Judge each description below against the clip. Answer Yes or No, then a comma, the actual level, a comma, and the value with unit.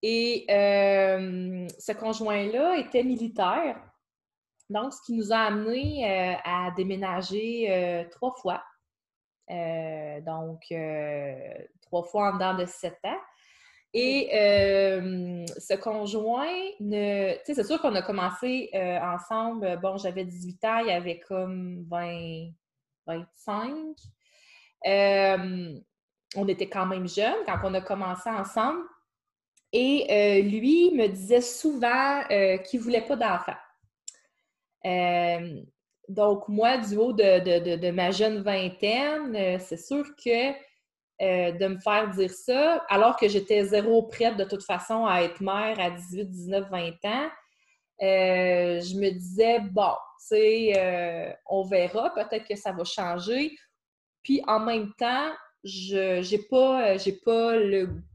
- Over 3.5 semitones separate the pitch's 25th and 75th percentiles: Yes, average, 4.1 semitones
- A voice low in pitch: No, high, 200 Hz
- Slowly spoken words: Yes, slow, 140 wpm